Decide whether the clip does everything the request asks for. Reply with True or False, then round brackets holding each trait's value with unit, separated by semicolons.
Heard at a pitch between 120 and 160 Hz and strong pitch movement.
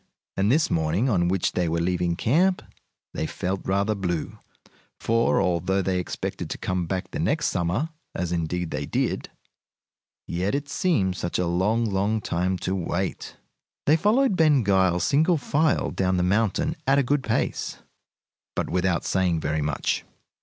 False (95 Hz; 6.6 semitones)